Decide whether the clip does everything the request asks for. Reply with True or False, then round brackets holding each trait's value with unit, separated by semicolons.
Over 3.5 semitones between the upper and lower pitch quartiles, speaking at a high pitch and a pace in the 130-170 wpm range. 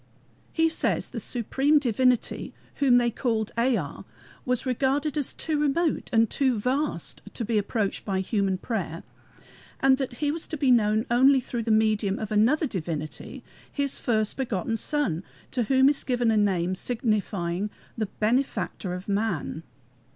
True (4.5 semitones; 235 Hz; 155 wpm)